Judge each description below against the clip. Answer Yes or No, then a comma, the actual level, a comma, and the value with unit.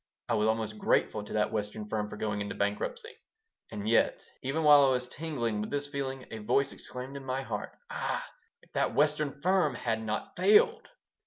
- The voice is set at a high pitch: No, low, 125 Hz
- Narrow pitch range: No, average, 5.1 semitones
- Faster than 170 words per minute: Yes, average, 190 wpm